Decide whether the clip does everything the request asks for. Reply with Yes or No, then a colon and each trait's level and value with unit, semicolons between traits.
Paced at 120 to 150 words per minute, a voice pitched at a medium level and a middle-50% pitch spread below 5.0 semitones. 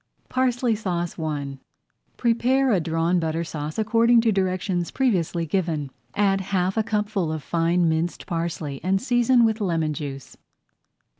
No: average, 140 wpm; medium, 180 Hz; average, 5.3 semitones